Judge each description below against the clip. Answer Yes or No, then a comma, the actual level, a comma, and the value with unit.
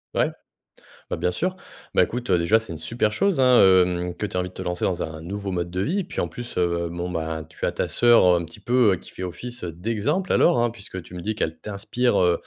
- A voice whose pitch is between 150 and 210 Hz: No, very low, 95 Hz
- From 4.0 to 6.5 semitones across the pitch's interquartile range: Yes, average, 5.2 semitones